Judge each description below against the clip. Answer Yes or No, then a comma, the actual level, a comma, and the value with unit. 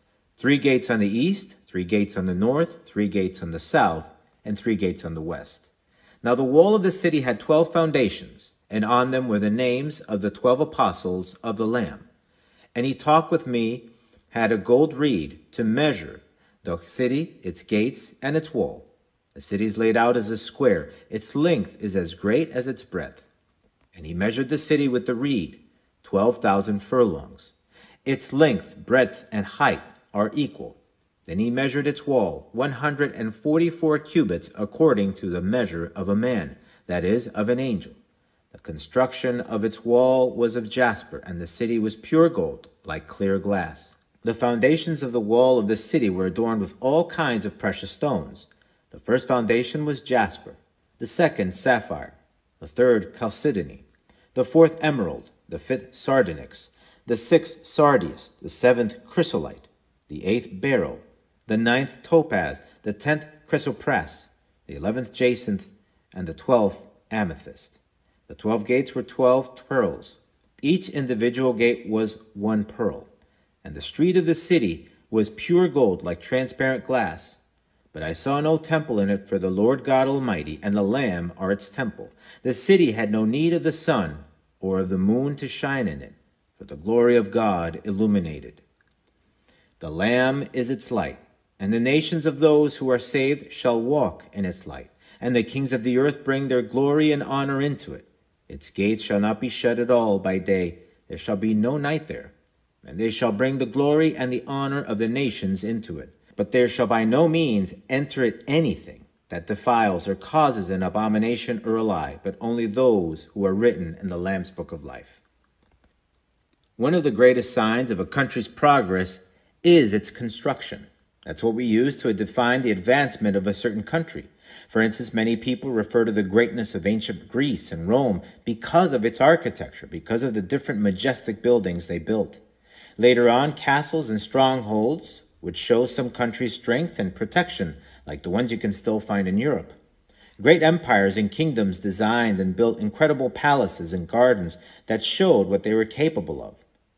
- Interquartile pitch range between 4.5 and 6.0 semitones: Yes, average, 5.2 semitones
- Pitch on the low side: Yes, low, 120 Hz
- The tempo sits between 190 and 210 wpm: No, average, 175 wpm